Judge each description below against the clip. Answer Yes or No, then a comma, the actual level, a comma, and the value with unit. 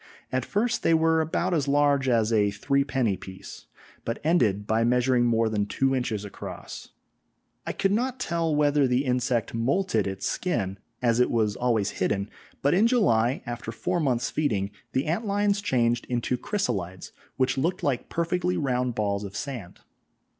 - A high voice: No, low, 125 Hz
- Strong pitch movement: Yes, wide, 6.2 semitones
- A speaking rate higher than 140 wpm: Yes, average, 165 wpm